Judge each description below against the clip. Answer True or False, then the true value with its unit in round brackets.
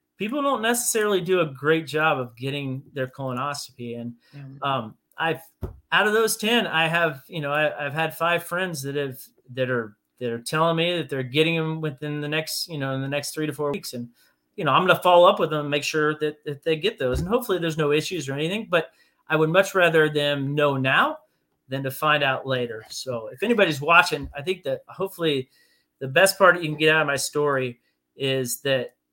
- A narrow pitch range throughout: False (3.9 semitones)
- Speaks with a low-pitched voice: False (150 Hz)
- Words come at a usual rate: False (225 wpm)